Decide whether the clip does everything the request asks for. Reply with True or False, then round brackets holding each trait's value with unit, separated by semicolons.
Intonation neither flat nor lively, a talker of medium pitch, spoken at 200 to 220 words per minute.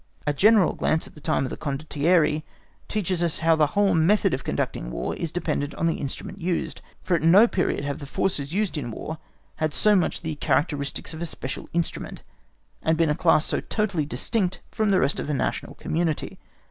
True (3.5 semitones; 160 Hz; 205 wpm)